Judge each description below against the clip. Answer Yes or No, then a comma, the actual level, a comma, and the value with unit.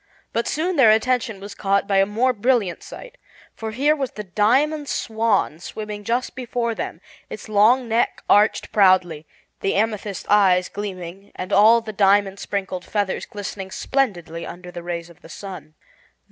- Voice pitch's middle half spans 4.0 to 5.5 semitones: No, average, 3.5 semitones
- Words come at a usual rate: Yes, average, 160 wpm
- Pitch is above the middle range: Yes, high, 205 Hz